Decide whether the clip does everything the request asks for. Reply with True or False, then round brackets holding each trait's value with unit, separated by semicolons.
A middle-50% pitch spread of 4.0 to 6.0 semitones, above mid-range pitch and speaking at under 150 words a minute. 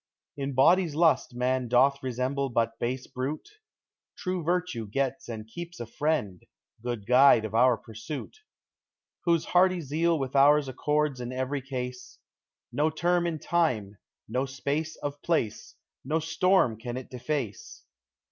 False (4.4 semitones; 135 Hz; 140 wpm)